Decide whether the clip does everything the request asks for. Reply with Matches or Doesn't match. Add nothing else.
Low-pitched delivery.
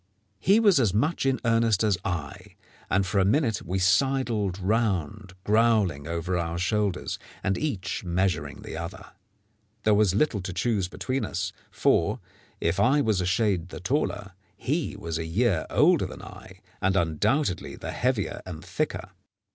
Matches